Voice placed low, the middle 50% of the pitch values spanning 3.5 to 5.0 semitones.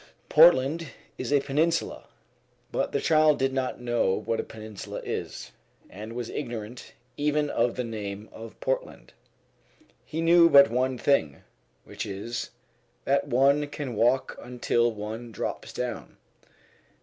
Yes: low, 125 Hz; average, 4.4 semitones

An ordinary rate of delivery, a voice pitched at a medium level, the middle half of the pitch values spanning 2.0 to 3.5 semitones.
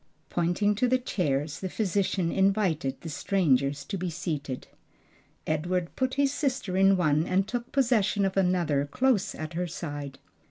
No: average, 155 wpm; medium, 180 Hz; average, 4.8 semitones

